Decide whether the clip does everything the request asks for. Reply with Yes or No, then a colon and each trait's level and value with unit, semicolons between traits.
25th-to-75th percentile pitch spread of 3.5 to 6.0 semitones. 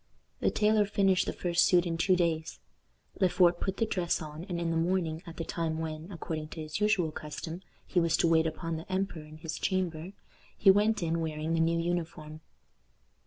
No: narrow, 2.5 semitones